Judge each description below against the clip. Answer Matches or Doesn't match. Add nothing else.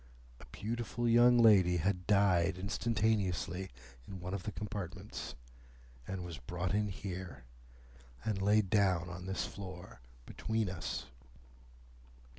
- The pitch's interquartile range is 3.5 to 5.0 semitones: Doesn't match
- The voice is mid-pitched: Doesn't match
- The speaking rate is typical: Doesn't match